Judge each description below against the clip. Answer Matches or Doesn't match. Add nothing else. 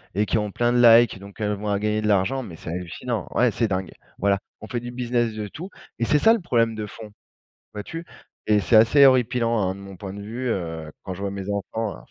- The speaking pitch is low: Matches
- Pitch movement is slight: Doesn't match